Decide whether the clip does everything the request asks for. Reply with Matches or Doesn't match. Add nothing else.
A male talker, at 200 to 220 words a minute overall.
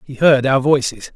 Matches